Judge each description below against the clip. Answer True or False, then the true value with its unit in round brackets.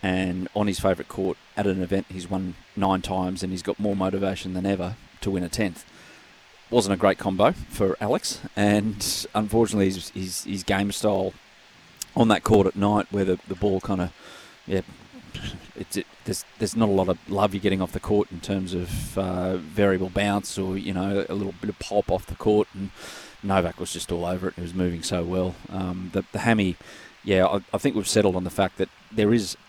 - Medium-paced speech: False (220 wpm)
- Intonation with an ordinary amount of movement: False (1.7 semitones)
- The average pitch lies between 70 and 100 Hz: True (95 Hz)